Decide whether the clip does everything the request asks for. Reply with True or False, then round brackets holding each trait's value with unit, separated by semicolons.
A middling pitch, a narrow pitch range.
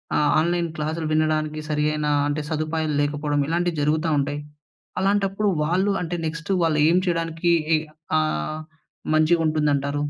True (155 Hz; 1.9 semitones)